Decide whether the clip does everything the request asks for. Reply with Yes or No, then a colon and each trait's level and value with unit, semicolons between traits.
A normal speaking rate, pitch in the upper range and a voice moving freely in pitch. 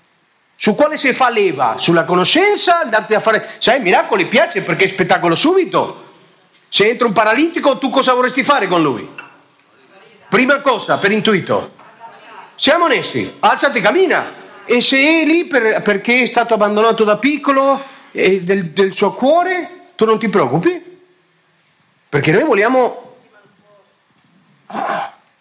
Yes: average, 135 wpm; high, 245 Hz; wide, 6.6 semitones